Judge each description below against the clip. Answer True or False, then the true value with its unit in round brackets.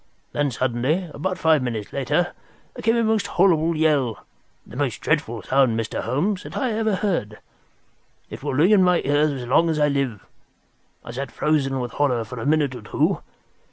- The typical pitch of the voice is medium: True (145 Hz)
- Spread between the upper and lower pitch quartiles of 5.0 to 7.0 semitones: True (5.6 semitones)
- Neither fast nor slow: True (185 wpm)